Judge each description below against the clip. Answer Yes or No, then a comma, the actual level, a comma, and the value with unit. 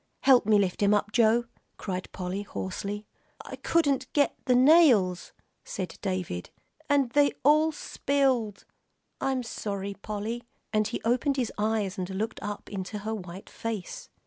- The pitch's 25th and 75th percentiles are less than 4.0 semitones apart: No, average, 4.6 semitones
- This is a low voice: No, high, 215 Hz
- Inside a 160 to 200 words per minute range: No, average, 150 wpm